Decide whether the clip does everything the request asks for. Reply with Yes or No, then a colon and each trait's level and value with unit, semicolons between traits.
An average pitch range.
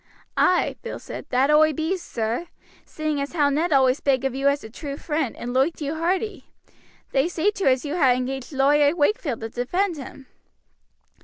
Yes: average, 3.5 semitones